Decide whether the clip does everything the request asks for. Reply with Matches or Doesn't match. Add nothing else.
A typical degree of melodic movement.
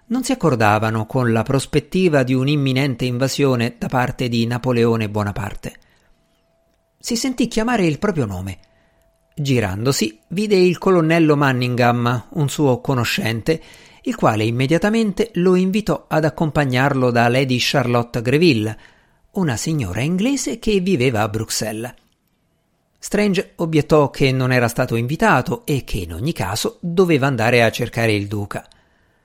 Doesn't match